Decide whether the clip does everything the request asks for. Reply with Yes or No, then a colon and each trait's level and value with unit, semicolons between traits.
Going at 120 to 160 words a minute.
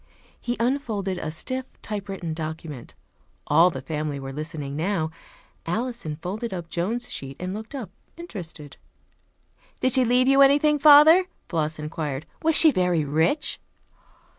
Yes: average, 140 wpm